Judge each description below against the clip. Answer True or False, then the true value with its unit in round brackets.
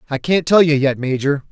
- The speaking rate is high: True (240 wpm)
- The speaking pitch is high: False (145 Hz)